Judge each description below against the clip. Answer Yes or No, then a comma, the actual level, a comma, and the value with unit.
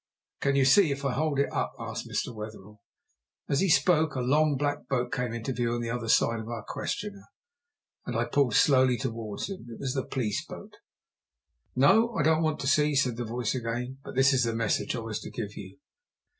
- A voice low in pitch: Yes, low, 130 Hz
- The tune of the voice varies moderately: Yes, average, 3.7 semitones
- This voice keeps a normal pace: No, fast, 210 wpm